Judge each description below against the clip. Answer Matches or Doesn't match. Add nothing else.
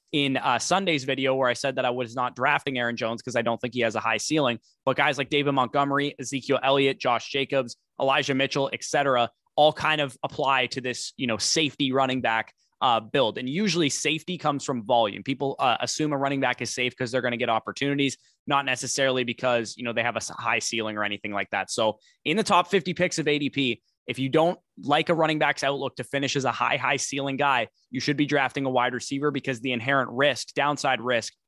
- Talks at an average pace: Doesn't match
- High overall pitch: Doesn't match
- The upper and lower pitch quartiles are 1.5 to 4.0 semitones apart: Matches